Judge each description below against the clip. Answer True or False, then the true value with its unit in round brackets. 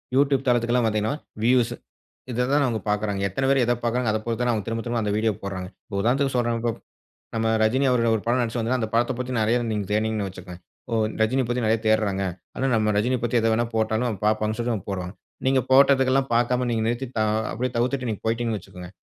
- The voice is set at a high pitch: False (115 Hz)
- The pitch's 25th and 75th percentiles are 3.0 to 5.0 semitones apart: False (2.4 semitones)